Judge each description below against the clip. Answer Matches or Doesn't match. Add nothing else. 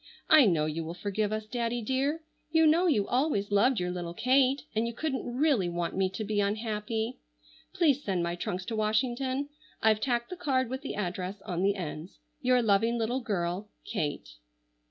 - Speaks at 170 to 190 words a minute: Matches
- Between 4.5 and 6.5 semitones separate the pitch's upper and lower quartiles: Matches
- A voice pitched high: Matches